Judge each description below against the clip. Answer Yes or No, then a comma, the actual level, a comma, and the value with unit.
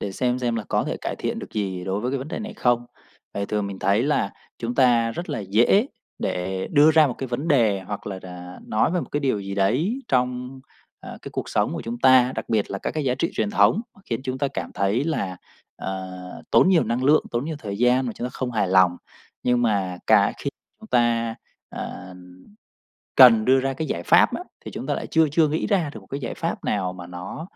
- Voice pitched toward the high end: No, low, 120 Hz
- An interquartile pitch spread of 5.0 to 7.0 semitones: Yes, wide, 5.4 semitones